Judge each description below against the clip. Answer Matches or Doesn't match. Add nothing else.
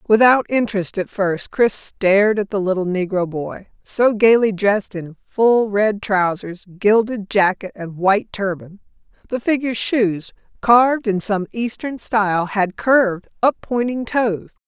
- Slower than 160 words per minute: Matches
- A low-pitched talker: Doesn't match